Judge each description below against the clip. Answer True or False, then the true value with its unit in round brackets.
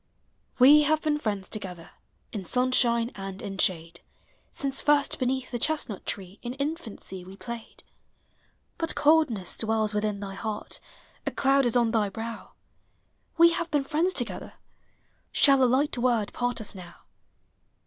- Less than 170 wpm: True (150 wpm)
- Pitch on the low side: False (235 Hz)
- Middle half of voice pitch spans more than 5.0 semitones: True (5.5 semitones)